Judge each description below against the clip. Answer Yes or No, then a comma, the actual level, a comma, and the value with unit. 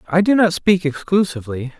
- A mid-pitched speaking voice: Yes, medium, 170 Hz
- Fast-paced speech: No, average, 165 wpm